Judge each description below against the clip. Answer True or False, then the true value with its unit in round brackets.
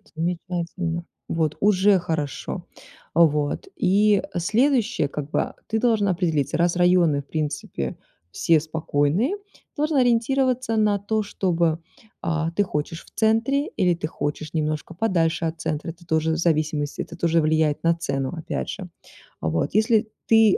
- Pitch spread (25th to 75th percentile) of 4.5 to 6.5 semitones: True (5.1 semitones)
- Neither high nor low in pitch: True (170 Hz)